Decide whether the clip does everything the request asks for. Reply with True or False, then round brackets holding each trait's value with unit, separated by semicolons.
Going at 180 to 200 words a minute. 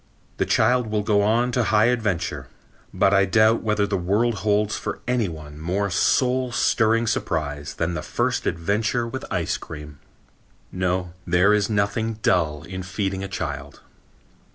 False (155 wpm)